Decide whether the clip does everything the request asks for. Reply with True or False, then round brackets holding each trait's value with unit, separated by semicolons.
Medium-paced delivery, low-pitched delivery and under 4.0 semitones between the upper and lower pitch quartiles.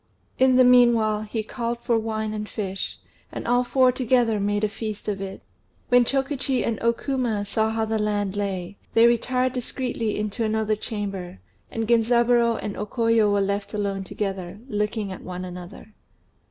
False (170 wpm; 220 Hz; 2.7 semitones)